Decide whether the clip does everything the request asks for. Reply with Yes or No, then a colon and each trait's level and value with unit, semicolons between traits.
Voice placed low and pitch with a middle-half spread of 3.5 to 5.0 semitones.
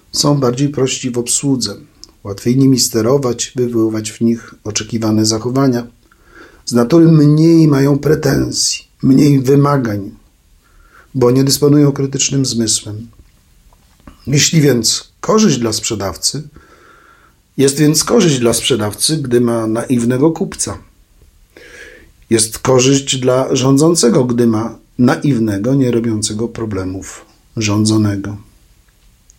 Yes: low, 120 Hz; average, 3.8 semitones